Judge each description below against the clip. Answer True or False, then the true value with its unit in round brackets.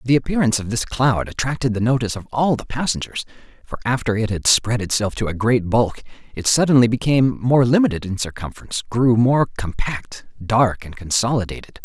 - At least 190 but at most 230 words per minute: False (175 wpm)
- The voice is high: False (115 Hz)